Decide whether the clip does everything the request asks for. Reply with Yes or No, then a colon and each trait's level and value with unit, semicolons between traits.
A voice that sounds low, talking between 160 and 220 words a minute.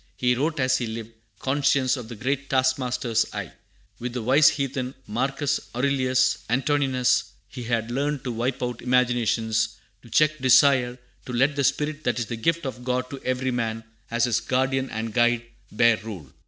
Yes: low, 125 Hz; average, 180 wpm